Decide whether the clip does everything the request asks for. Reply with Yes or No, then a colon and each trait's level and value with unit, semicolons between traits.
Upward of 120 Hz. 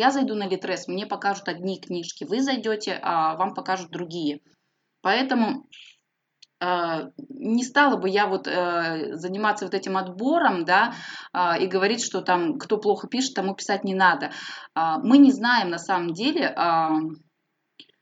Yes: high, 190 Hz